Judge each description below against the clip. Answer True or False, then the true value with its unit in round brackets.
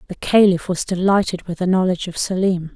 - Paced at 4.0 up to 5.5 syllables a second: False (5.9 syllables/s)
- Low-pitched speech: False (185 Hz)